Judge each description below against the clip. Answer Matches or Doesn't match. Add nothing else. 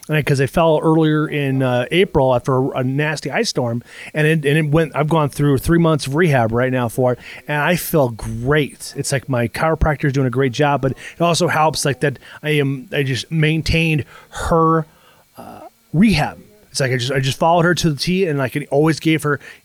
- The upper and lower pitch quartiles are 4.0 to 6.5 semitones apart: Doesn't match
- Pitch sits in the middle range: Matches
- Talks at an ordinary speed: Doesn't match